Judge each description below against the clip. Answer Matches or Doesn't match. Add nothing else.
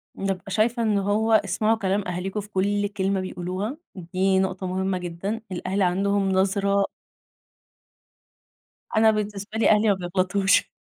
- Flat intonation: Matches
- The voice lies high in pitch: Matches